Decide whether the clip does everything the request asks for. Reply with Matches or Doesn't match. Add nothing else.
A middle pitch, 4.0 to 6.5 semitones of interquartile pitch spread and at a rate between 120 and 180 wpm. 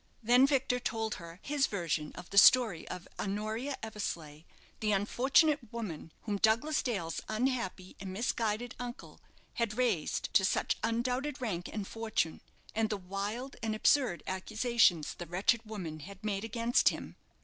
Doesn't match